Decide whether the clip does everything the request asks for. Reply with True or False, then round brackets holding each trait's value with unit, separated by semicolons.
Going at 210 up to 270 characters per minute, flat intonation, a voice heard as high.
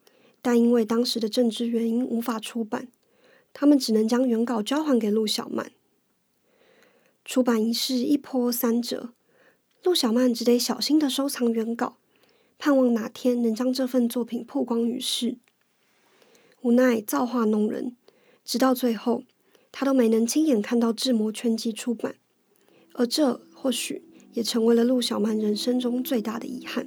True (230 characters per minute; 1.9 semitones; 245 Hz)